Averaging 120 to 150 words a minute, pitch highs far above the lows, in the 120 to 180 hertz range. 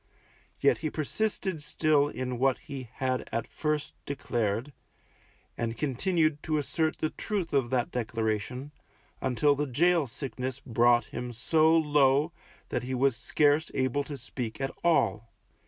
No: average, 140 wpm; average, 3.8 semitones; low, 135 Hz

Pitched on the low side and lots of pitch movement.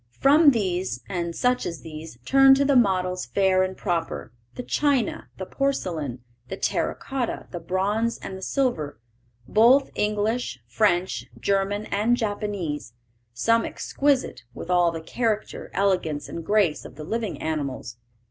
No: high, 195 Hz; wide, 5.7 semitones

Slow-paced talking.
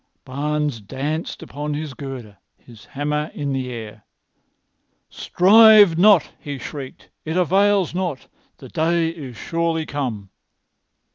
Yes: slow, 120 wpm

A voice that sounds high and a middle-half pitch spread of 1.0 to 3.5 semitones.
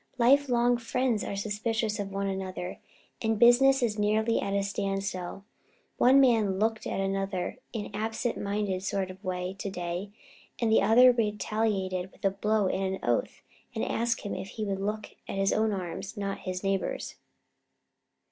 Yes: high, 205 Hz; narrow, 2.5 semitones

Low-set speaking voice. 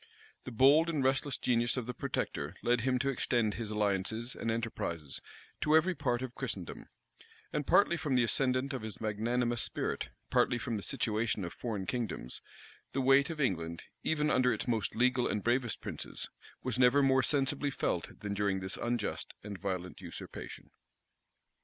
Yes: low, 120 Hz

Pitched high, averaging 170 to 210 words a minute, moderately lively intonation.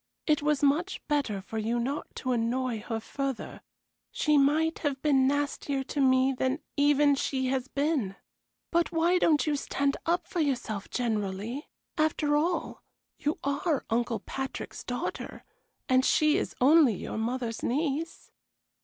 No: very high, 275 Hz; average, 145 wpm; average, 3.3 semitones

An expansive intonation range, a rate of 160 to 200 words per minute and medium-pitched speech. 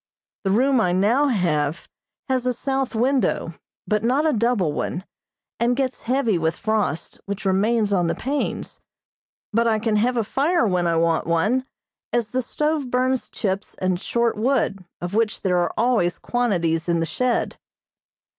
No: wide, 5.7 semitones; average, 165 wpm; high, 220 Hz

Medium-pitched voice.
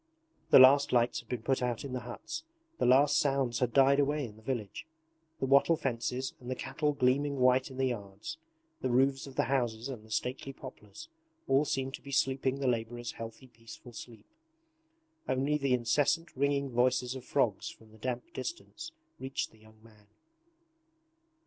No: low, 130 Hz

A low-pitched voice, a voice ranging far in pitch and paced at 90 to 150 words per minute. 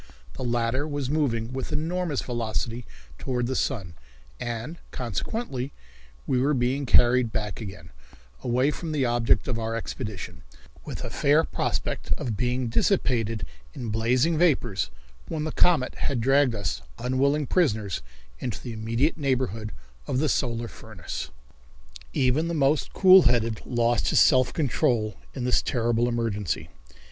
No: low, 125 Hz; average, 3.6 semitones; average, 140 wpm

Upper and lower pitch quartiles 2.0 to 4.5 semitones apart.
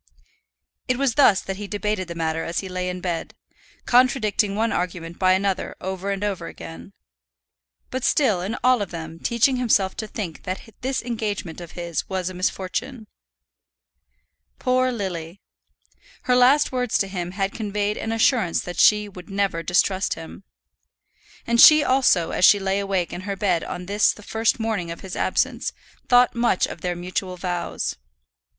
Yes: average, 3.9 semitones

